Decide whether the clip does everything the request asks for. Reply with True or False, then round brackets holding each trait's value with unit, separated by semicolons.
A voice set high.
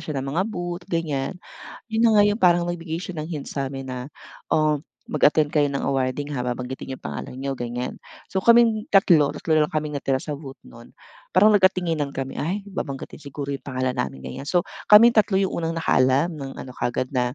False (150 Hz)